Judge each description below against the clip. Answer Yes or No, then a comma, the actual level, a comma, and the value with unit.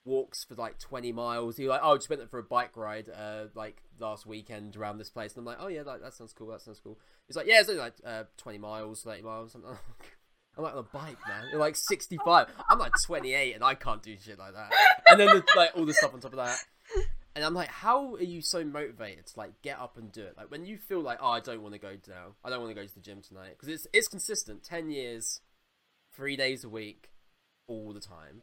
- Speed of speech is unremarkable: No, fast, 265 wpm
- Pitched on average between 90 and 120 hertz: Yes, low, 115 Hz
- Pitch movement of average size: No, wide, 7.1 semitones